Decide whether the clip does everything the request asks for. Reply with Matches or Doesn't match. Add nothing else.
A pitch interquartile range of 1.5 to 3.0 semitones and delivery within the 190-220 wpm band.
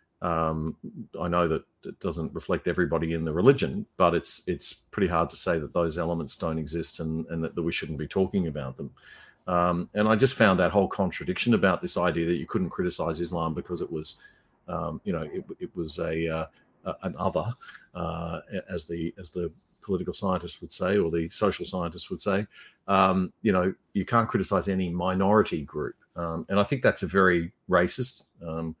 Matches